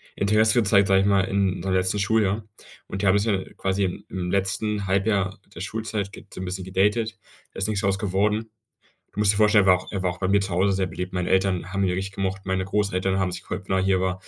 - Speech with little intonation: Yes, narrow, 1.5 semitones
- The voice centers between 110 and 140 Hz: No, very low, 95 Hz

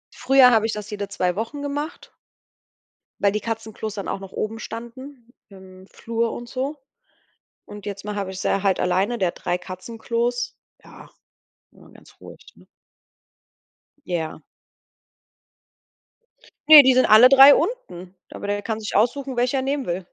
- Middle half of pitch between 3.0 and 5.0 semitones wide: Yes, average, 4.6 semitones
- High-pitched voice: Yes, high, 220 Hz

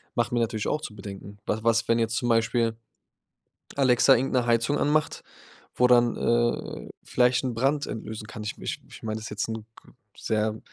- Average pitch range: No, narrow, 2.0 semitones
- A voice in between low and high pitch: No, low, 115 Hz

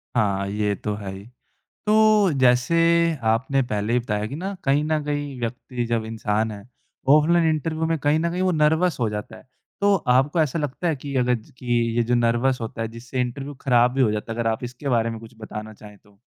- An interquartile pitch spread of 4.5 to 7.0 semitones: Yes, average, 5.0 semitones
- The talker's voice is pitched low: Yes, low, 125 Hz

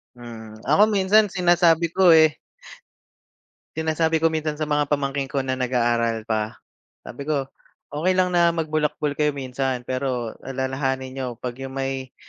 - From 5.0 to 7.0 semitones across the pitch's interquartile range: No, average, 3.6 semitones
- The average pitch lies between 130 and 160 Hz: Yes, medium, 140 Hz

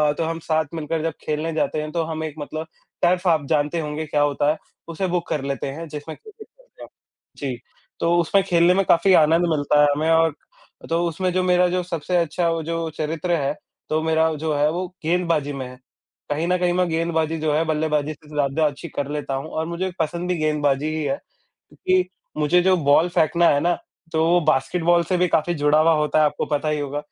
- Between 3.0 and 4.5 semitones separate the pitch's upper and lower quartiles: No, narrow, 2.5 semitones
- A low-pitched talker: No, medium, 160 Hz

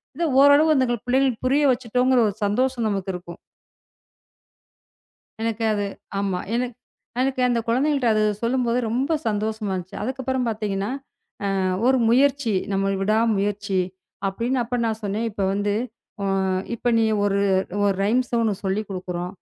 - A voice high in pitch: Yes, high, 225 Hz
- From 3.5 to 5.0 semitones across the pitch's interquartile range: Yes, average, 4.1 semitones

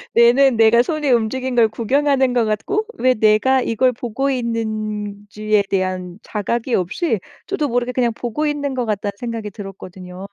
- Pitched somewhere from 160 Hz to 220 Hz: No, high, 230 Hz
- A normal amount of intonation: Yes, average, 3.6 semitones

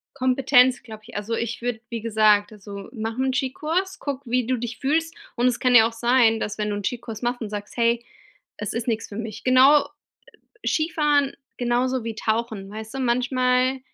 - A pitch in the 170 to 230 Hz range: No, high, 240 Hz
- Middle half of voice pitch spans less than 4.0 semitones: Yes, average, 2.8 semitones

